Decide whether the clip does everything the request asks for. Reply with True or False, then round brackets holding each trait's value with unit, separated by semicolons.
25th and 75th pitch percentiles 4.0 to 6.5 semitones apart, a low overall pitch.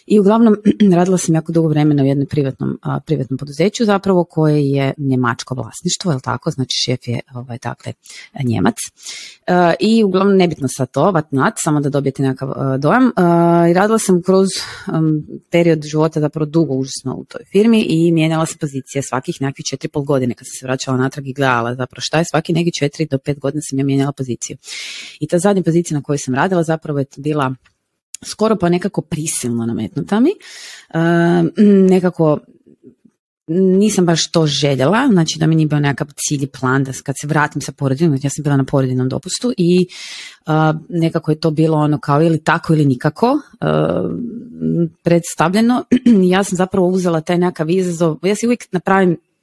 False (4.5 semitones; 155 Hz)